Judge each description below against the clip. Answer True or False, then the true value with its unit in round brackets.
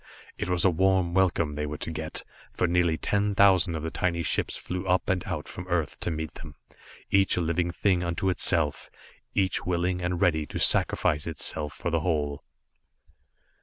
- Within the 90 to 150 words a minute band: False (185 wpm)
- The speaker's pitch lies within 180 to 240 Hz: False (85 Hz)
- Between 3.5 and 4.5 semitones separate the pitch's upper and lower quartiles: False (2.5 semitones)